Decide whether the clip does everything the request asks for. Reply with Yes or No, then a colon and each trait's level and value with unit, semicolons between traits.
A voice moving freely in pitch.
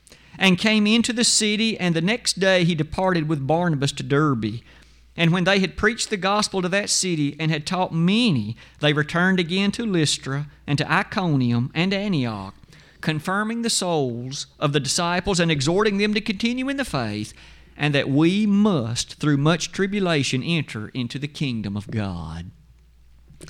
Yes: wide, 6.2 semitones